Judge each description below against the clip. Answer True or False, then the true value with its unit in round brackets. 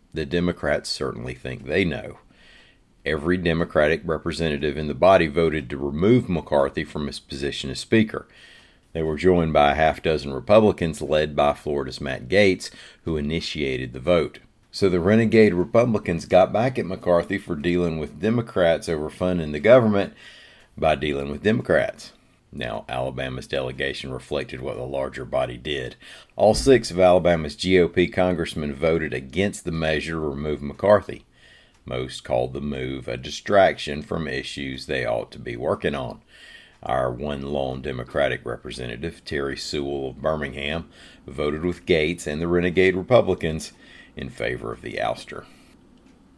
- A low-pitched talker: True (80 Hz)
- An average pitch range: True (3.9 semitones)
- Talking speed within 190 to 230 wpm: False (150 wpm)